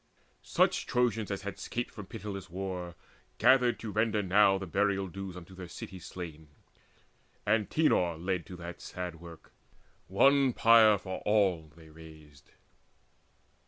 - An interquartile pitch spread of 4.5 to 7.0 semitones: No, average, 3.5 semitones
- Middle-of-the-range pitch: No, very low, 95 Hz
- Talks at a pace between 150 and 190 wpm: No, slow, 135 wpm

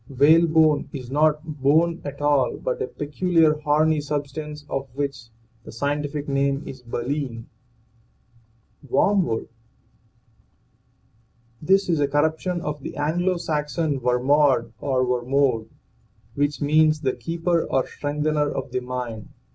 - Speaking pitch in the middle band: Yes, medium, 145 Hz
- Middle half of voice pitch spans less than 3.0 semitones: Yes, narrow, 2.5 semitones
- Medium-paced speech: No, slow, 120 wpm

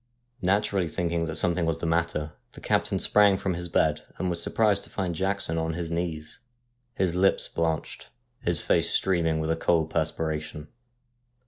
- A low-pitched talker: Yes, very low, 85 Hz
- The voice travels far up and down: No, narrow, 2.4 semitones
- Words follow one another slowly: No, average, 165 wpm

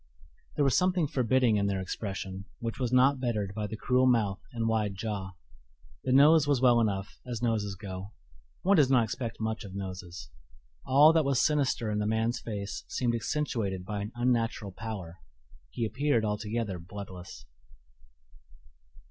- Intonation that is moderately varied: Yes, average, 4.2 semitones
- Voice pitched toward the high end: No, low, 110 Hz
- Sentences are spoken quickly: No, average, 160 wpm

